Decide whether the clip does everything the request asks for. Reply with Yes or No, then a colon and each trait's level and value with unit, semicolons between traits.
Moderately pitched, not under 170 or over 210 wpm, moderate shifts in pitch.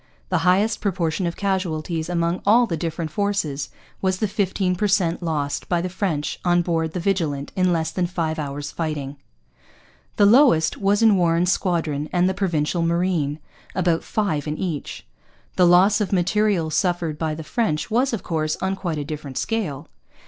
Yes: medium, 175 Hz; average, 175 wpm; average, 3.5 semitones